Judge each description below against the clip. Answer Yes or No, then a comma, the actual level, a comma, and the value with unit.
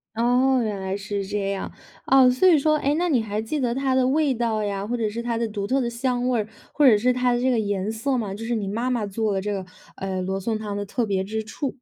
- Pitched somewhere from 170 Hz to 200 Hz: No, high, 225 Hz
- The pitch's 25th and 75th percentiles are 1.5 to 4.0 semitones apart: Yes, average, 3.7 semitones